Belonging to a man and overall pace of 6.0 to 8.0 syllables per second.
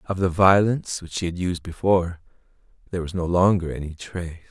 Yes: male; 6.2 syllables/s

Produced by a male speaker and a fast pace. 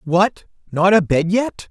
No: male; average, 140 wpm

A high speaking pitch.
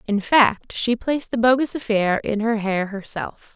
Yes: high, 225 Hz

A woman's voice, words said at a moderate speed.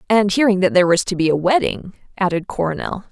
No: female; fast, 210 wpm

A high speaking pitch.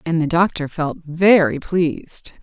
No: medium, 165 Hz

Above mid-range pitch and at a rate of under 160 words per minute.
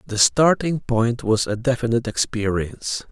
No: low, 120 Hz; slow, 135 wpm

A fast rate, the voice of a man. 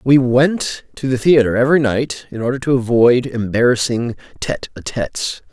No: average, 165 wpm; male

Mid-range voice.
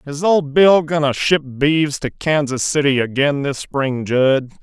Yes: medium, 145 Hz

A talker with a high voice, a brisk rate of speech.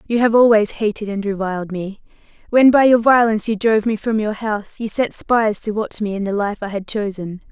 Yes: high, 215 Hz; fast, 230 wpm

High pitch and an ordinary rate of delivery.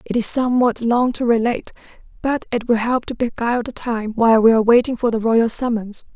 No: high, 235 Hz; fast, 215 wpm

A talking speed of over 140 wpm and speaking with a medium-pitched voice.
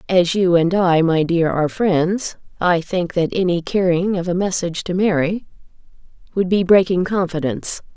Yes: average, 165 wpm; medium, 175 Hz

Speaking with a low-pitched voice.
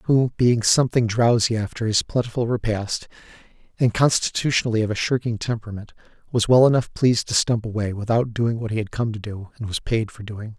Yes: low, 115 Hz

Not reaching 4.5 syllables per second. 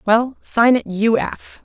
Yes: 3.5 syllables/s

